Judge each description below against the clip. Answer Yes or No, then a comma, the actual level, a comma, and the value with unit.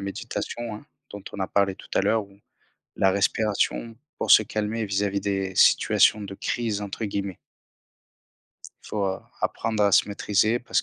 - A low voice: Yes, low, 100 Hz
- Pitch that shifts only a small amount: Yes, narrow, 1.8 semitones